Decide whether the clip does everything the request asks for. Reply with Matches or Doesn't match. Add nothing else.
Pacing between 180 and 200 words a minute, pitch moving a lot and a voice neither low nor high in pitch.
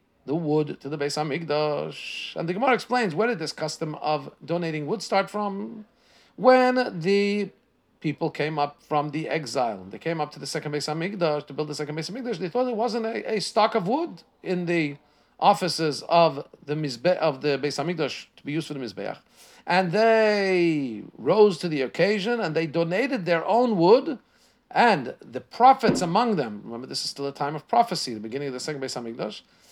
Matches